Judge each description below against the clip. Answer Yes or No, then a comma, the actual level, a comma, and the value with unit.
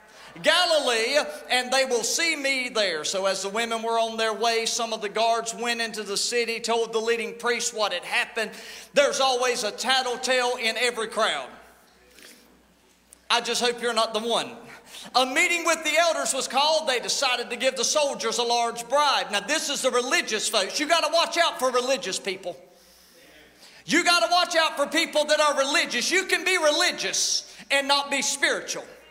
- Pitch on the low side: No, high, 245 Hz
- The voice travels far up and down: No, average, 4.5 semitones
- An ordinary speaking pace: Yes, average, 190 wpm